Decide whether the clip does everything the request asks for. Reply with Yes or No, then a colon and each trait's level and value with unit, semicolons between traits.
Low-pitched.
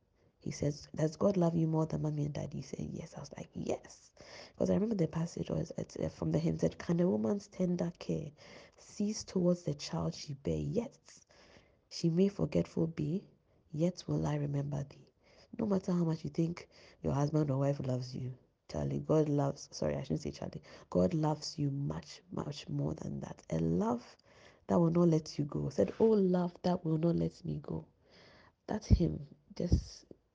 No: medium, 155 Hz